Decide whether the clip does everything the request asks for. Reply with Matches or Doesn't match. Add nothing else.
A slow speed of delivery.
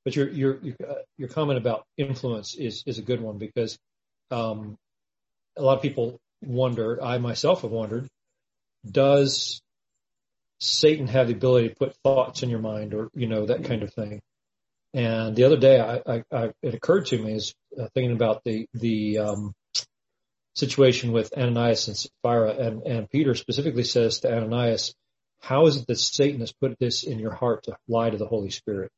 Doesn't match